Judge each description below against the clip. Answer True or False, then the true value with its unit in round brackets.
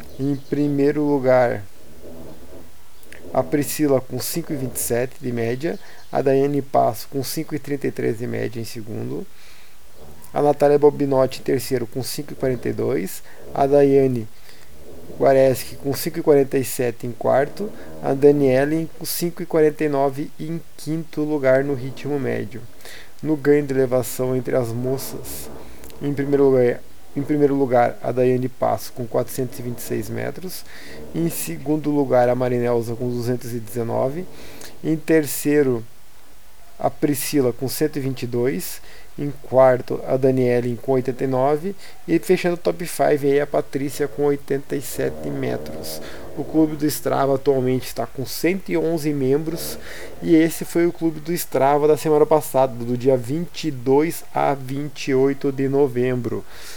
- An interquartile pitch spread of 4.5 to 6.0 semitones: False (3.3 semitones)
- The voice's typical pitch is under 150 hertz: True (135 Hz)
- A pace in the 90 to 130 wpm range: True (125 wpm)